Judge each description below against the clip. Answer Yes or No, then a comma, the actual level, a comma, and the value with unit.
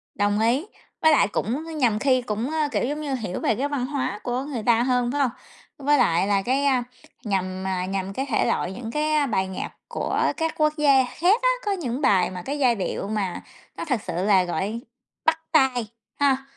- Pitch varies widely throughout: Yes, wide, 6.0 semitones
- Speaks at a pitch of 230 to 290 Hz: Yes, very high, 250 Hz